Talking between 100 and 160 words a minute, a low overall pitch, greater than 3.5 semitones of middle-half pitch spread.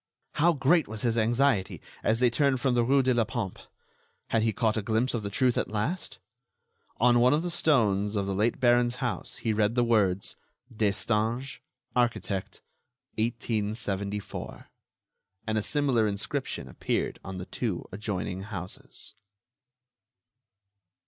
No: average, 145 wpm; low, 115 Hz; average, 3.2 semitones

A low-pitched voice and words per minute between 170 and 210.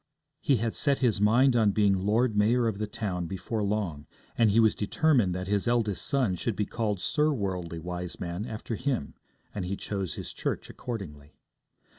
Yes: low, 105 Hz; average, 180 wpm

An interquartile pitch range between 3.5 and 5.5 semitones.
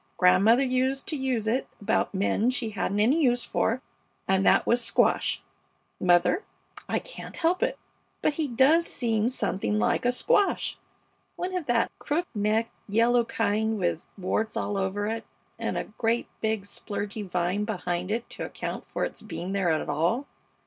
Yes: average, 4.2 semitones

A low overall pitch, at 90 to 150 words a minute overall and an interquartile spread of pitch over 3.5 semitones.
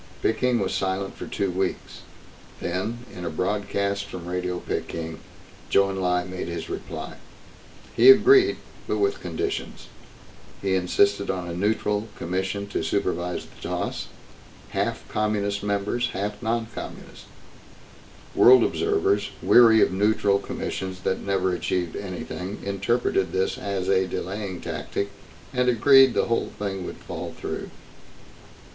No: low, 100 Hz; slow, 135 wpm; average, 3.2 semitones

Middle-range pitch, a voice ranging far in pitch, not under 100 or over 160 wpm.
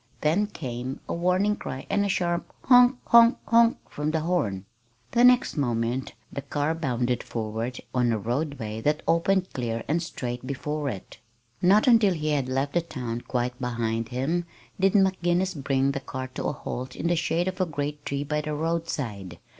No: medium, 145 Hz; wide, 5.9 semitones; average, 180 wpm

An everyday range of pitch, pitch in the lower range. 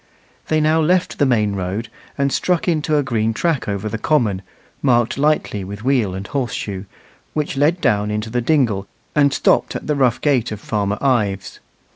No: wide, 6.0 semitones; low, 120 Hz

